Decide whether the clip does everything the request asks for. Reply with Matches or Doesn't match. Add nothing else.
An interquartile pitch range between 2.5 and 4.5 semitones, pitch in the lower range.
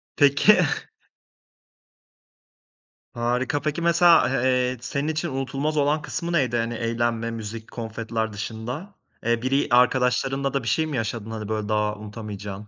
Matches